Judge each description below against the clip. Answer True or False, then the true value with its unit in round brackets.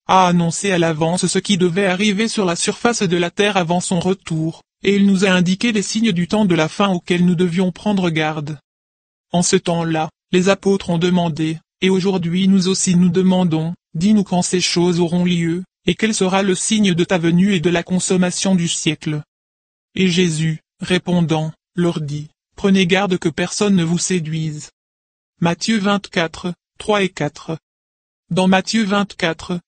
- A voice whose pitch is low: False (180 Hz)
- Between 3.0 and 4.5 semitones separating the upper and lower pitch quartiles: False (2.5 semitones)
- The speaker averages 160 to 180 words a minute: True (175 wpm)